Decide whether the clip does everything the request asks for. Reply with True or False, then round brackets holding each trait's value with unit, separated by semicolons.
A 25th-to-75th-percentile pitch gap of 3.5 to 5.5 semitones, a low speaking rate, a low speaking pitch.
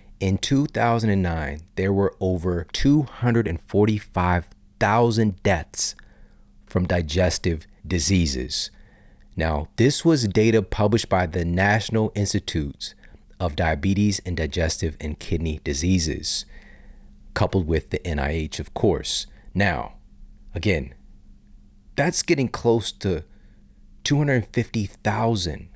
True (4.1 semitones; 90 wpm; 95 Hz)